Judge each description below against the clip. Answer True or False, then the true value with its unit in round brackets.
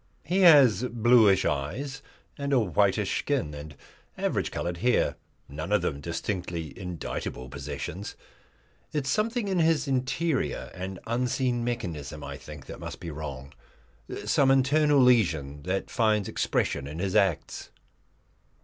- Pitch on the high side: False (100 Hz)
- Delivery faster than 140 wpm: False (135 wpm)